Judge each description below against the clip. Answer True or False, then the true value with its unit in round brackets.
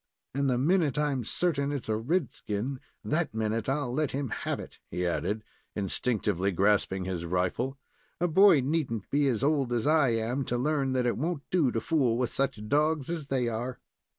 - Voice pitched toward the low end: True (130 Hz)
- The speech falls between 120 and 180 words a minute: False (195 wpm)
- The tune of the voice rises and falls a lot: False (4.8 semitones)